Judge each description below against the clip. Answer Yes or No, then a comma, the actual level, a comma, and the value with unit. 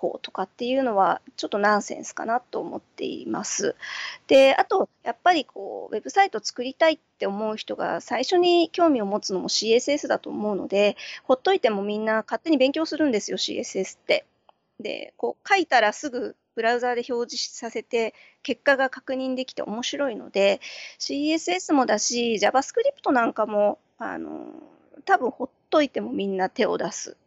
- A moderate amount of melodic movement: No, wide, 6.3 semitones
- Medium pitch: No, very high, 260 Hz